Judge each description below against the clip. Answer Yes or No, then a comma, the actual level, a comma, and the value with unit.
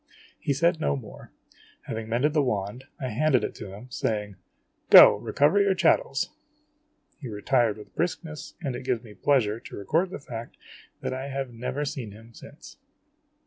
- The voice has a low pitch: Yes, low, 130 Hz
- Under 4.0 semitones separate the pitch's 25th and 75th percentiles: No, average, 4.9 semitones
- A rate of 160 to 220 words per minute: Yes, average, 180 wpm